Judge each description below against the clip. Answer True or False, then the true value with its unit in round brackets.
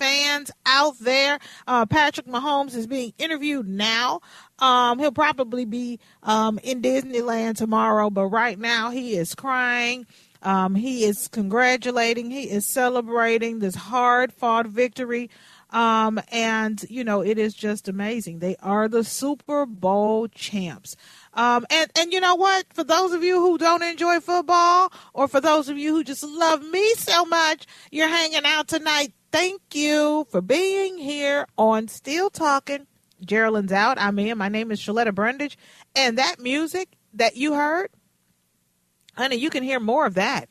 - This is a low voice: False (250 Hz)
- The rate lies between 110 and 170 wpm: True (160 wpm)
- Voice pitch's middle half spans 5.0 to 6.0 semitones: True (5.4 semitones)